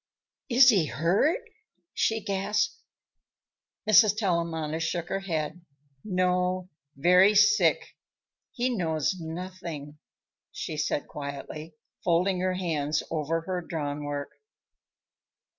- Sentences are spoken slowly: Yes, slow, 100 wpm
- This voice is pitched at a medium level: Yes, medium, 175 Hz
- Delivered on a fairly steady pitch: No, average, 3.7 semitones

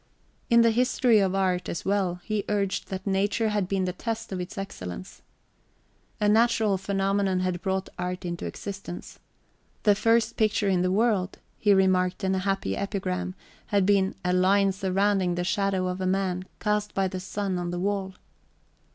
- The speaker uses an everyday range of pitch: No, narrow, 1.8 semitones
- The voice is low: No, high, 195 Hz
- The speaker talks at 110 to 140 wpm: No, average, 175 wpm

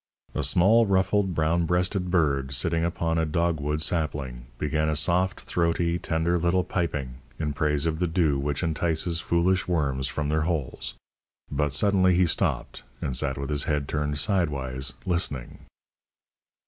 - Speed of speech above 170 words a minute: No, average, 155 wpm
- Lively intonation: No, average, 3.2 semitones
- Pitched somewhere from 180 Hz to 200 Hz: No, very low, 80 Hz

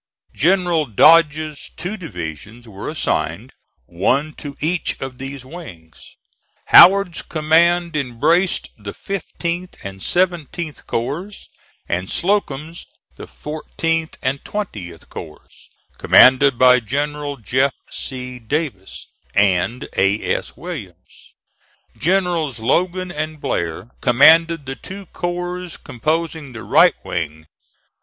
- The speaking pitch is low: No, medium, 150 Hz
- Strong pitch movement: Yes, wide, 6.4 semitones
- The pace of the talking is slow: Yes, slow, 105 wpm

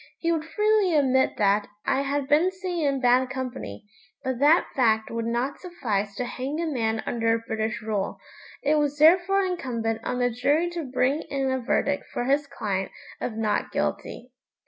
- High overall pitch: Yes, very high, 260 Hz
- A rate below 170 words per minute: No, average, 175 wpm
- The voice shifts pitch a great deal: No, average, 5.0 semitones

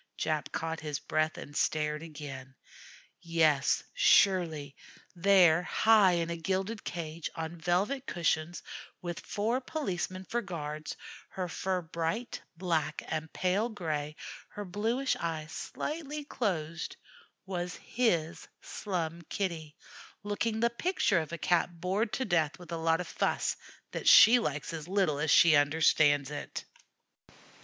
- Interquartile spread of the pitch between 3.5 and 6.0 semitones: Yes, average, 4.2 semitones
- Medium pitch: Yes, medium, 170 Hz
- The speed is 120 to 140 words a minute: Yes, slow, 135 wpm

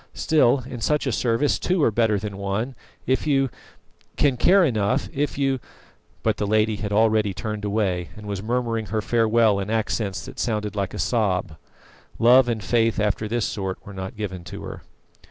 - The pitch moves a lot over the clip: No, average, 3.1 semitones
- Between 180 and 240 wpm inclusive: Yes, average, 190 wpm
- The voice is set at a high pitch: No, low, 110 Hz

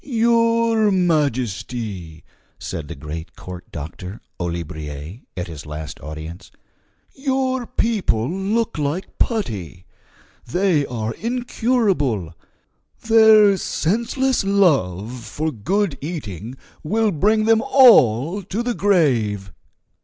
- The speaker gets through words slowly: Yes, slow, 100 wpm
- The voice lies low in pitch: No, medium, 150 Hz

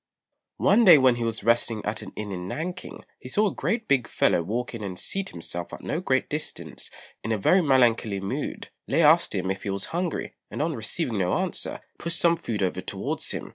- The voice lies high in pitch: No, low, 120 Hz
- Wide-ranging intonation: Yes, wide, 8.6 semitones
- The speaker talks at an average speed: No, fast, 215 wpm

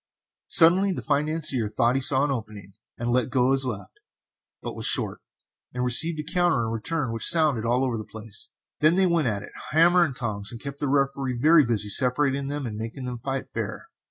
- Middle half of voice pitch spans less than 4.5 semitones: No, average, 4.8 semitones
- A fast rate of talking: Yes, fast, 210 wpm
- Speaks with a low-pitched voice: Yes, low, 130 Hz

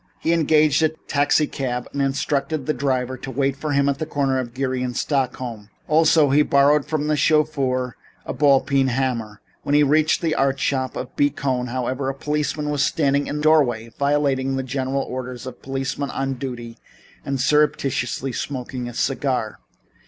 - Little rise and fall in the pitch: Yes, narrow, 2.3 semitones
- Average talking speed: Yes, average, 180 wpm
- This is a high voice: No, low, 135 Hz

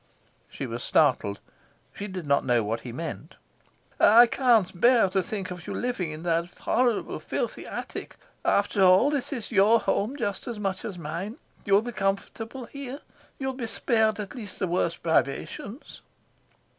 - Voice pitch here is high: Yes, high, 200 Hz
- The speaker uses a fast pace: No, average, 165 wpm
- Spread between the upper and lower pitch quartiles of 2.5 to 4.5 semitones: No, average, 5.2 semitones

